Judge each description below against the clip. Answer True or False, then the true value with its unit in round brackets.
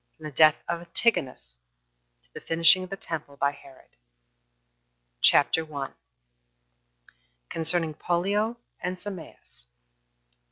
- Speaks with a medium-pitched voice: True (165 Hz)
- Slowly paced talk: True (110 wpm)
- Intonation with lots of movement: False (4.1 semitones)